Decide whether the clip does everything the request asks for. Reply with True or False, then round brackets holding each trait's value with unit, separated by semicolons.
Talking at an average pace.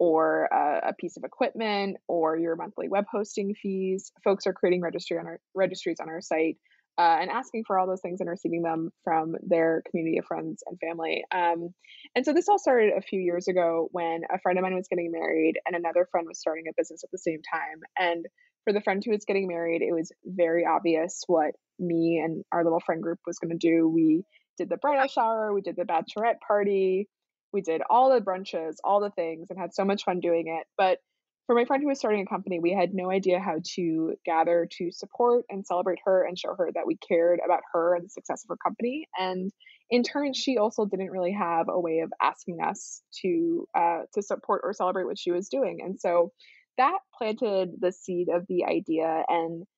False (220 wpm)